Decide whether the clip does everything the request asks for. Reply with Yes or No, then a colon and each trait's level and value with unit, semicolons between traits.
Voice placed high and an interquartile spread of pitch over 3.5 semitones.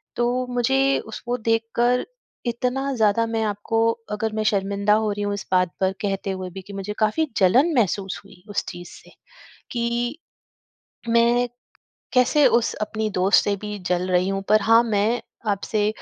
No: high, 215 Hz; average, 3.2 semitones